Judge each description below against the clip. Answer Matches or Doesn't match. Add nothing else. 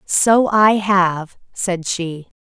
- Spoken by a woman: Matches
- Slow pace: Matches